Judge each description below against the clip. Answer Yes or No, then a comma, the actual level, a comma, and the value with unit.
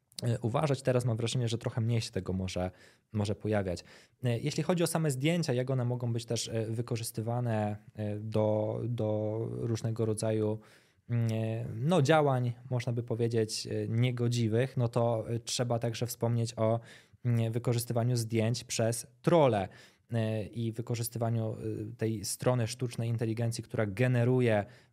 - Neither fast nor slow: Yes, average, 125 wpm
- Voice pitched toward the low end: Yes, low, 115 Hz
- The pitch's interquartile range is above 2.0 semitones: No, narrow, 1.7 semitones